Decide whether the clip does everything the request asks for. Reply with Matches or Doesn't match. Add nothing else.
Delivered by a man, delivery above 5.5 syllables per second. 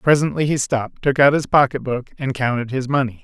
Matches